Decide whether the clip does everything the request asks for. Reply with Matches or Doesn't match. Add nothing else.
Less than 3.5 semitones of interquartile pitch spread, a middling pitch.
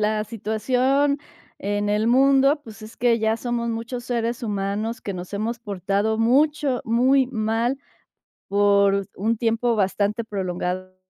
Doesn't match